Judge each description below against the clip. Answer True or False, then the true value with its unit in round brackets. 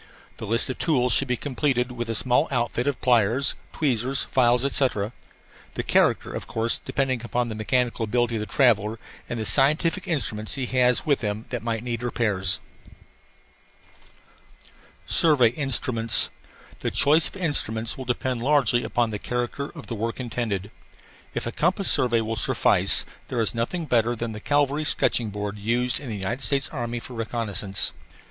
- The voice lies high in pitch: False (120 Hz)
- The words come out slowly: False (165 wpm)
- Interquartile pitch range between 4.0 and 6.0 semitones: False (2.9 semitones)